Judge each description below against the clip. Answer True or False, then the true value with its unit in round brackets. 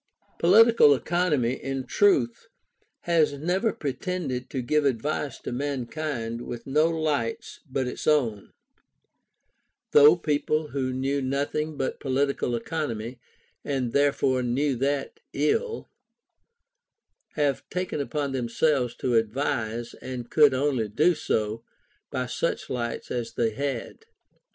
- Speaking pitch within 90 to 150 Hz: True (140 Hz)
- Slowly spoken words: True (115 wpm)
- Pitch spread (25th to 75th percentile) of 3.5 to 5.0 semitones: True (3.8 semitones)